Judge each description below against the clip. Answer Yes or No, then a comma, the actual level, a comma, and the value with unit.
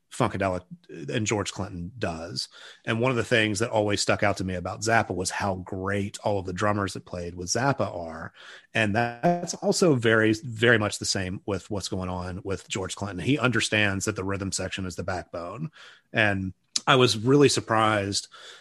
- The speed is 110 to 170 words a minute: No, average, 190 wpm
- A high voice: No, low, 105 Hz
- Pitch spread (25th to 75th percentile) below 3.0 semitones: No, average, 3.6 semitones